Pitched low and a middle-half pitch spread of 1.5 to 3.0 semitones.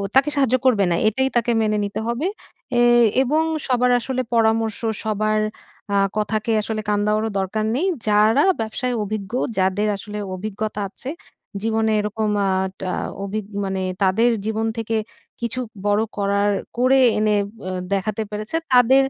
No: high, 220 Hz; narrow, 2.5 semitones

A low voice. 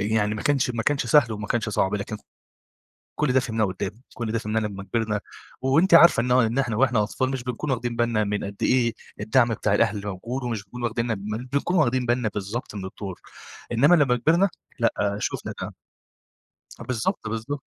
Yes: low, 115 Hz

